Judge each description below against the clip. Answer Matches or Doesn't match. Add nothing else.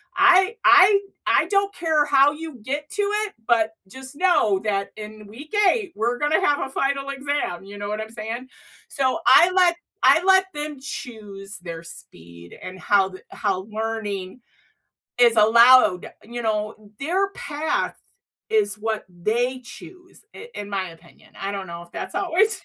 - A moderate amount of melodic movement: Doesn't match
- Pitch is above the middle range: Matches